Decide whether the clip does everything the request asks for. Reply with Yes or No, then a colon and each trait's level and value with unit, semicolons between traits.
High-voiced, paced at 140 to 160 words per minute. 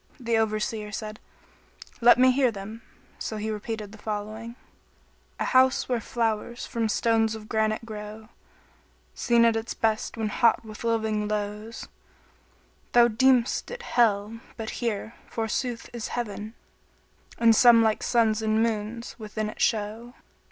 Yes: high, 225 Hz; average, 145 wpm